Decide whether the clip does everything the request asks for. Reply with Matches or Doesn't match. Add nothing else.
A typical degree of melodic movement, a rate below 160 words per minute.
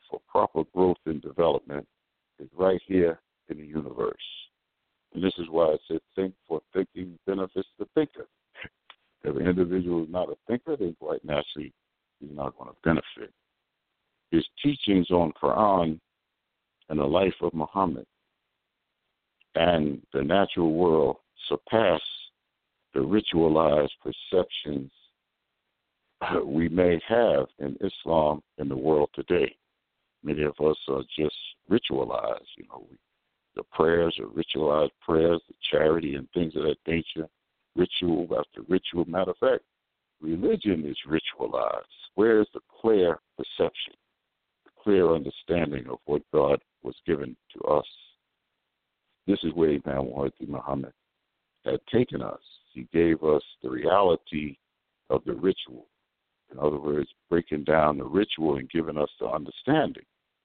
Matches